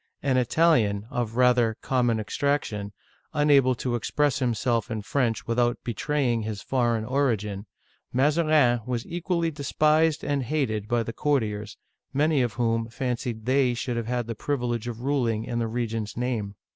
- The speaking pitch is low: Yes, low, 120 Hz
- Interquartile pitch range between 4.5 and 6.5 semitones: No, average, 3.6 semitones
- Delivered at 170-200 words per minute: No, average, 155 wpm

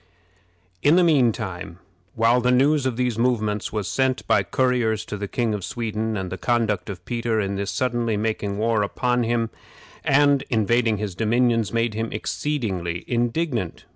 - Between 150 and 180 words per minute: Yes, average, 165 wpm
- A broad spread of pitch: No, average, 2.9 semitones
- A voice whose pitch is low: Yes, low, 115 Hz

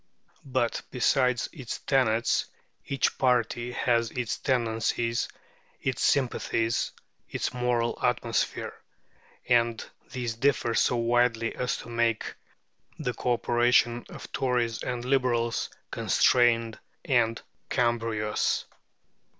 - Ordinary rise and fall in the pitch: No, narrow, 1.3 semitones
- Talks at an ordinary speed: No, slow, 100 wpm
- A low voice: Yes, low, 120 Hz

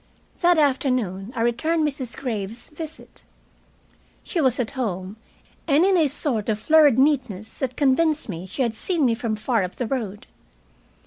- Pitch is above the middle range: Yes, very high, 255 Hz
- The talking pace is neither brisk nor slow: Yes, average, 165 wpm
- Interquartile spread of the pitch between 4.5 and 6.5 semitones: Yes, wide, 5.4 semitones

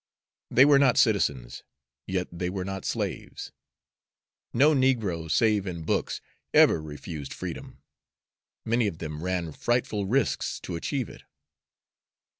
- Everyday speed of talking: No, slow, 125 wpm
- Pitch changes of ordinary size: No, wide, 6.3 semitones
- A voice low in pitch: Yes, very low, 95 Hz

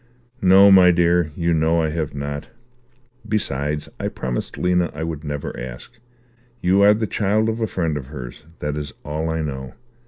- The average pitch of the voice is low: Yes, very low, 80 Hz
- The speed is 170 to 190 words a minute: Yes, average, 180 wpm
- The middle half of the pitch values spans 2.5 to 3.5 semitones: No, average, 4.0 semitones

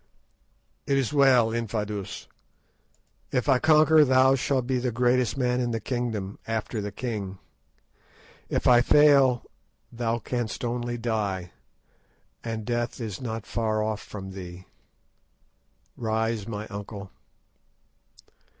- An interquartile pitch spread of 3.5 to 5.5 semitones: No, average, 2.8 semitones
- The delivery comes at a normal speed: No, slow, 120 wpm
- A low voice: Yes, low, 115 Hz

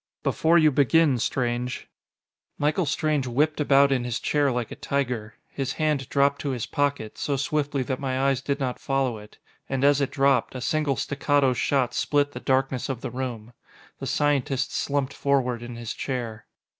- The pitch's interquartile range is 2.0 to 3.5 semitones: Yes, narrow, 2.4 semitones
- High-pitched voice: No, low, 135 Hz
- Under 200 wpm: Yes, average, 180 wpm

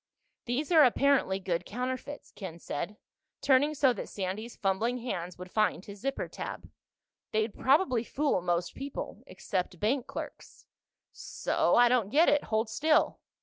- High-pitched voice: Yes, high, 230 Hz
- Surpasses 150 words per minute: No, average, 145 wpm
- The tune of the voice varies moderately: No, wide, 6.1 semitones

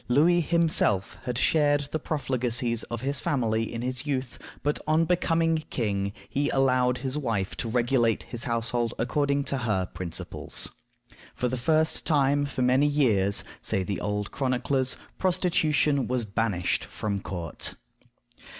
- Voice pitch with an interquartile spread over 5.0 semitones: No, average, 4.2 semitones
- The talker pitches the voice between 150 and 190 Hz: No, low, 125 Hz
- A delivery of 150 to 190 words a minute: No, average, 140 wpm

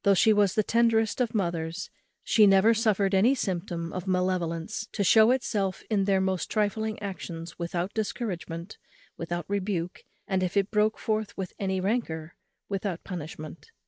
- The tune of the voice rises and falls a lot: No, average, 3.7 semitones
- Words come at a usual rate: Yes, average, 155 wpm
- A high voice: Yes, high, 195 Hz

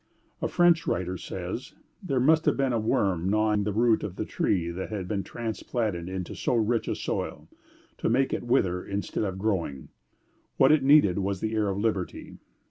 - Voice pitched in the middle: No, low, 105 Hz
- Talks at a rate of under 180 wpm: No, average, 190 wpm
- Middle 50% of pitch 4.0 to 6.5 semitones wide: Yes, average, 4.3 semitones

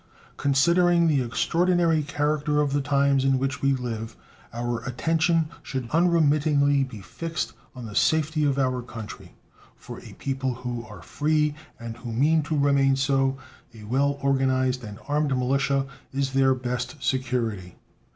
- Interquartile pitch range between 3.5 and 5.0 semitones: No, average, 2.9 semitones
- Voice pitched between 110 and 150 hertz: Yes, low, 135 Hz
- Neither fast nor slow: Yes, average, 150 wpm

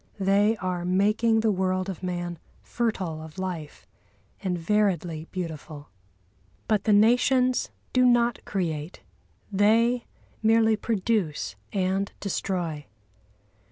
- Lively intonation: No, average, 4.1 semitones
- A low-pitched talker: No, high, 195 Hz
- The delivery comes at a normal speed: No, slow, 105 wpm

